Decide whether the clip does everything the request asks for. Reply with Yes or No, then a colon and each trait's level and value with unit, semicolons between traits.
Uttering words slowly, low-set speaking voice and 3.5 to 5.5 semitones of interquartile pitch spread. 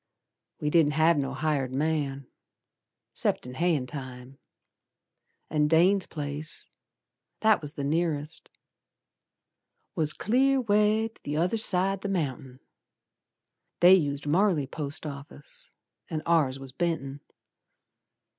No: slow, 110 wpm; medium, 155 Hz; average, 4.1 semitones